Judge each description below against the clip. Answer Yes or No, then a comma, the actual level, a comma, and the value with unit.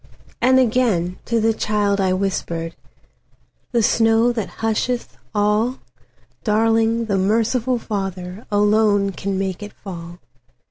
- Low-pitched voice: No, high, 210 Hz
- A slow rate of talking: Yes, slow, 100 wpm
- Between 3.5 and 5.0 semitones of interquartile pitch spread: No, average, 2.7 semitones